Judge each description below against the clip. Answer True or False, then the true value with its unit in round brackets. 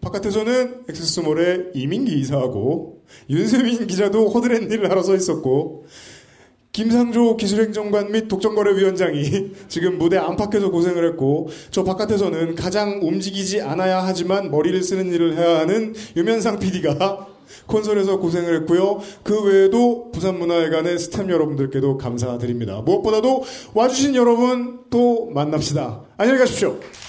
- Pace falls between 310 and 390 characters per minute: True (350 characters per minute)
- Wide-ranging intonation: False (4.7 semitones)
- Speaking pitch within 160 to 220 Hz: True (190 Hz)